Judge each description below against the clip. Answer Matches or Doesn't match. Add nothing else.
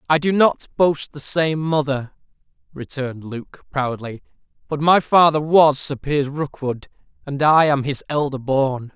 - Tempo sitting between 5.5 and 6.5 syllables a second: Doesn't match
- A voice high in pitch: Doesn't match